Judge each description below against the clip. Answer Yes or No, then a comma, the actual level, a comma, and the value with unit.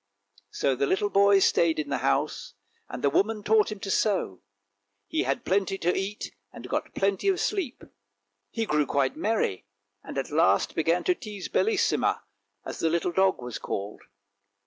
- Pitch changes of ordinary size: No, wide, 6.8 semitones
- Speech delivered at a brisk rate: No, average, 175 wpm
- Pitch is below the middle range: No, high, 190 Hz